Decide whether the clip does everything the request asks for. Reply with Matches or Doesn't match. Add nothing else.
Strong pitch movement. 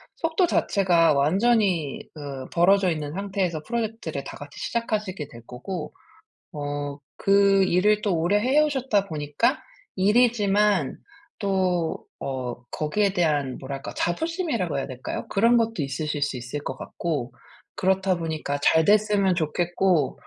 Matches